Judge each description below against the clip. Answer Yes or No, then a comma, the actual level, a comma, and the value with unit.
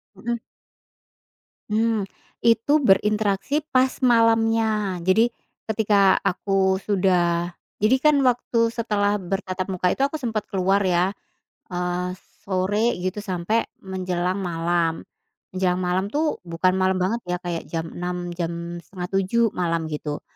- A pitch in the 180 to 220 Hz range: Yes, high, 190 Hz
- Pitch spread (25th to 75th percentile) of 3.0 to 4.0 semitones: Yes, average, 3.7 semitones